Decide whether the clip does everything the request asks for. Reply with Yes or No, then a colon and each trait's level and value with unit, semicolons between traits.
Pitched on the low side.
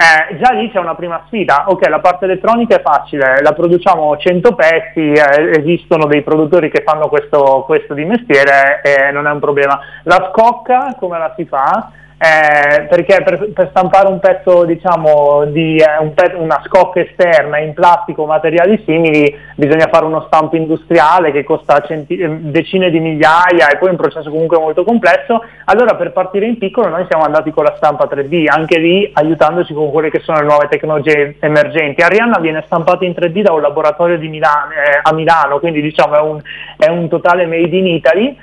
No: medium, 160 Hz